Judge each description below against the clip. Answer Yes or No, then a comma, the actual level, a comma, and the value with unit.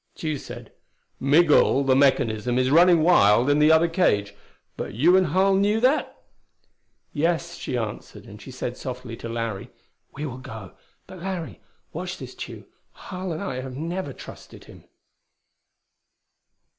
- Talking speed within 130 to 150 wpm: Yes, average, 145 wpm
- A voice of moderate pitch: Yes, medium, 150 Hz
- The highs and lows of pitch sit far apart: Yes, wide, 5.9 semitones